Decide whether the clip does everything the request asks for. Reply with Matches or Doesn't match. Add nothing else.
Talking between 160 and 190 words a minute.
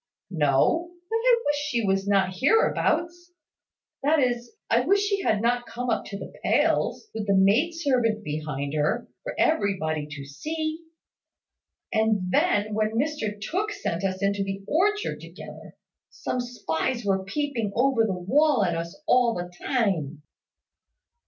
Doesn't match